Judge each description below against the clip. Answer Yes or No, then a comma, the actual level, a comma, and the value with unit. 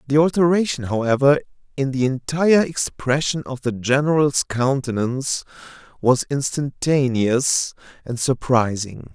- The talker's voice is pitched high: No, low, 135 Hz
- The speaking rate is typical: No, slow, 100 wpm